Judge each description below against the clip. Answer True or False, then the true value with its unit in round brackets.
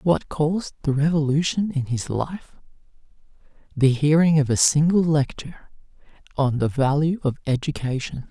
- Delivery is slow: True (130 wpm)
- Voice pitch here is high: False (150 Hz)